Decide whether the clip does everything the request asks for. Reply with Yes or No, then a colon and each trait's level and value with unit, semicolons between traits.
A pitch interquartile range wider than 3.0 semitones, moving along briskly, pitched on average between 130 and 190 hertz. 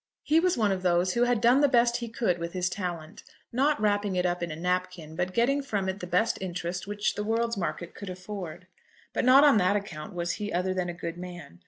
Yes: average, 4.5 semitones; fast, 240 wpm; medium, 185 Hz